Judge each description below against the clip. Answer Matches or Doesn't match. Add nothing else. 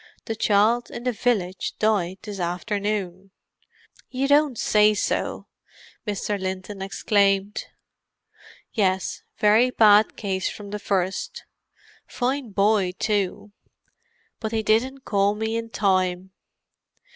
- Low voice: Doesn't match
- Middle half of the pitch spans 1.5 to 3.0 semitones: Matches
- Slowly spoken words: Matches